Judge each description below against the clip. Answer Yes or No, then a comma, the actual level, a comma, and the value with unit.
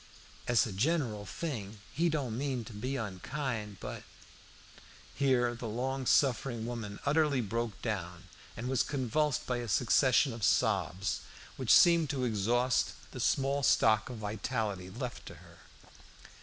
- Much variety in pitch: No, average, 4.0 semitones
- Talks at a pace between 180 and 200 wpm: No, average, 145 wpm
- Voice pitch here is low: Yes, low, 120 Hz